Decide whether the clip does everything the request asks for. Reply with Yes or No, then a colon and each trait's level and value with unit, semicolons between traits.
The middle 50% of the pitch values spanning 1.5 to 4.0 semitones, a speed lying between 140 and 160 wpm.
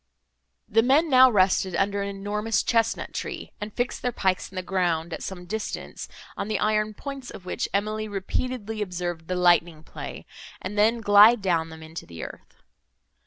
No: average, 3.5 semitones; average, 175 wpm